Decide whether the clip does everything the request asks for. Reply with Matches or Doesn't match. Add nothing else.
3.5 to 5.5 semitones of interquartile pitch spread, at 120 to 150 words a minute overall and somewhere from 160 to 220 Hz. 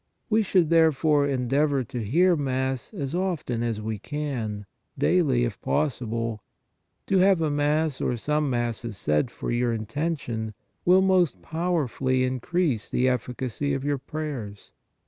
Doesn't match